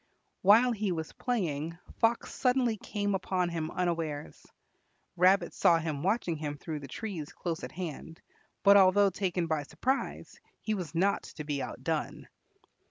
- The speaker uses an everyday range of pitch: Yes, average, 4.3 semitones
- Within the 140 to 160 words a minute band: Yes, average, 150 wpm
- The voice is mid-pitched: Yes, medium, 180 Hz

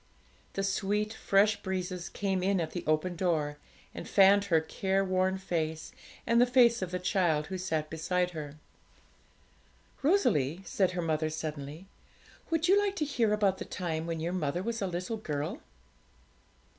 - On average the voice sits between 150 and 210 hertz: Yes, medium, 185 Hz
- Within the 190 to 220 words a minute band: No, average, 160 wpm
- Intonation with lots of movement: No, average, 4.0 semitones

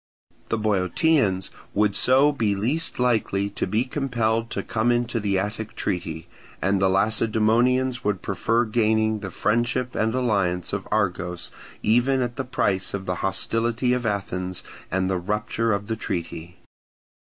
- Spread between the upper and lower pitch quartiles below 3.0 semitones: No, average, 3.7 semitones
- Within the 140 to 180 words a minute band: Yes, average, 150 wpm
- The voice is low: Yes, low, 110 Hz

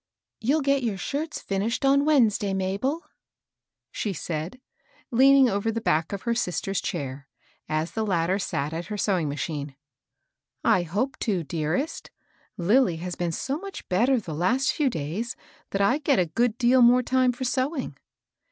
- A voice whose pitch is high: Yes, high, 210 Hz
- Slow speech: No, average, 175 wpm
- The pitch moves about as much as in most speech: No, wide, 7.0 semitones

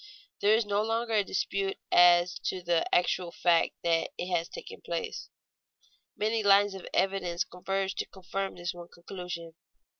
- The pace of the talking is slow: No, average, 155 wpm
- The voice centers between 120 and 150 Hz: No, high, 190 Hz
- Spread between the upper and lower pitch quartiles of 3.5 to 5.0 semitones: No, narrow, 2.5 semitones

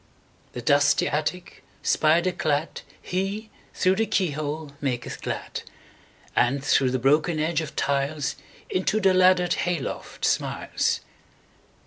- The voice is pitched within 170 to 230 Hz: No, medium, 155 Hz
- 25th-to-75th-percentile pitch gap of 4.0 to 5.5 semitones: Yes, average, 4.3 semitones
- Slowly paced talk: Yes, slow, 105 wpm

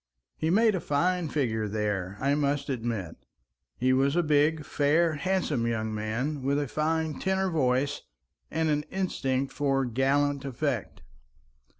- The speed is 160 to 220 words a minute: No, average, 140 wpm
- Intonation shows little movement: No, average, 3.8 semitones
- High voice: No, medium, 140 Hz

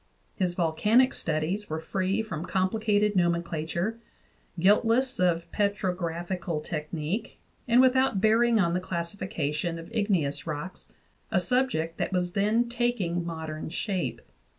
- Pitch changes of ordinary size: Yes, average, 4.5 semitones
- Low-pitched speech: No, medium, 185 Hz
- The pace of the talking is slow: Yes, slow, 120 wpm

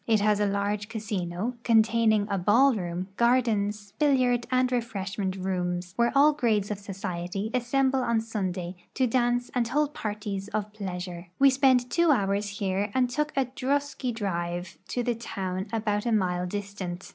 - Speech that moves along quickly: No, average, 160 wpm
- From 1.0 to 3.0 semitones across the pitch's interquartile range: No, average, 4.1 semitones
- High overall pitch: Yes, high, 210 Hz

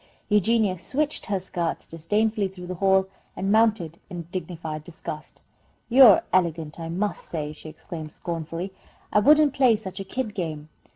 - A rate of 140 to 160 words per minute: Yes, average, 155 wpm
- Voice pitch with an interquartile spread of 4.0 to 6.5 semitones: Yes, average, 4.3 semitones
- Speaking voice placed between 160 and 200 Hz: Yes, medium, 185 Hz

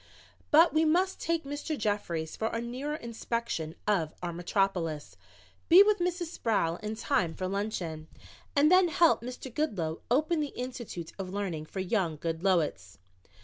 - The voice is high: Yes, high, 220 Hz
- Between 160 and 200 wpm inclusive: No, average, 150 wpm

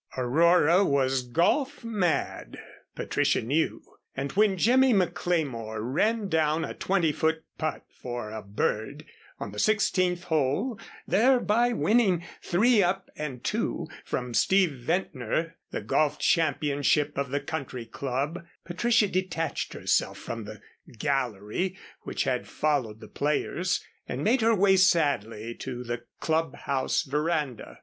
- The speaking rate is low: Yes, slow, 130 wpm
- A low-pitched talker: No, medium, 155 Hz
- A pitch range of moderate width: No, wide, 6.5 semitones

